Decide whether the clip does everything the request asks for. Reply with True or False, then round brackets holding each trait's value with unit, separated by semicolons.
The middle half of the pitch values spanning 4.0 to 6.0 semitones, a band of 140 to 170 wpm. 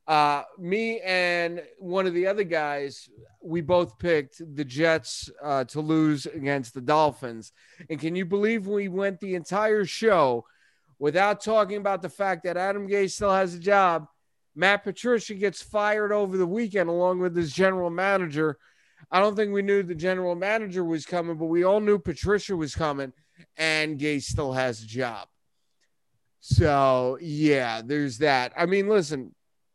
True (4.8 semitones; 165 wpm)